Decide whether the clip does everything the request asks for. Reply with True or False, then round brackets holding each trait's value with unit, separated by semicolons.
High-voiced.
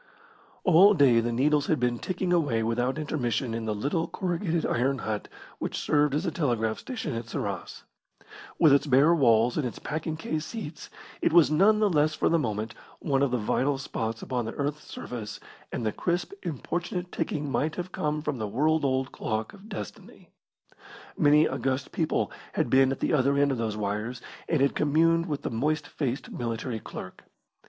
False (140 Hz)